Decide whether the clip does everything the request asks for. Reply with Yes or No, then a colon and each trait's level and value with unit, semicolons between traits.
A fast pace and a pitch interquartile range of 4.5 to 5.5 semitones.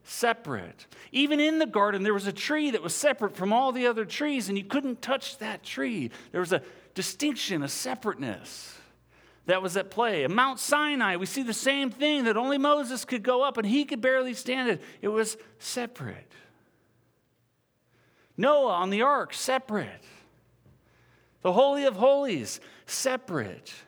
No: average, 165 wpm; average, 5.1 semitones